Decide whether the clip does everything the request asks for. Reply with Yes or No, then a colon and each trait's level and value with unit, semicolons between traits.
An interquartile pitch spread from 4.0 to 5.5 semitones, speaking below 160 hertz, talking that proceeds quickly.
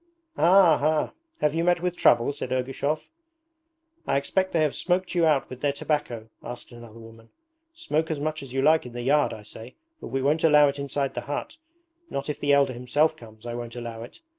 Yes: average, 4.4 semitones; medium, 140 Hz; fast, 215 wpm